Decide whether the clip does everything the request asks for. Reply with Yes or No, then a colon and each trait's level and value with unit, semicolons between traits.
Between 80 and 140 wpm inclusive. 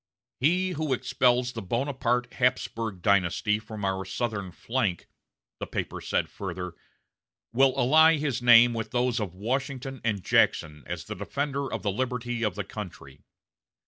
No: average, 150 wpm